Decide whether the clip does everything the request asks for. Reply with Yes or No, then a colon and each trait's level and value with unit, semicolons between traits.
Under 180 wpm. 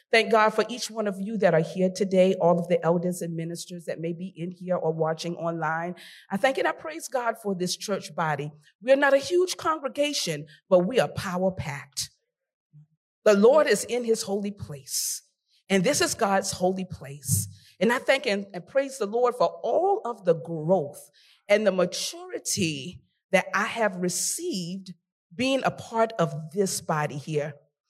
No: average, 185 wpm